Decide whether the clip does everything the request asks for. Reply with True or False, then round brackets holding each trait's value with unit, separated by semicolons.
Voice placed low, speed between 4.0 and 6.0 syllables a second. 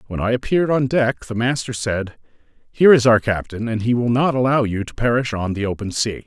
True (120 Hz; 5.8 syllables/s)